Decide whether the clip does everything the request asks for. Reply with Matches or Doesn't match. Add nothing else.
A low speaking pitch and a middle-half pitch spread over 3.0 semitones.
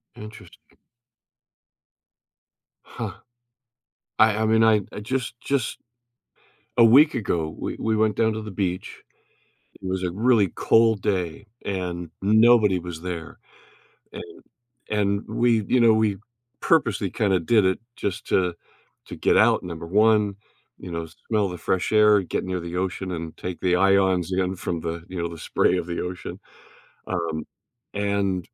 Matches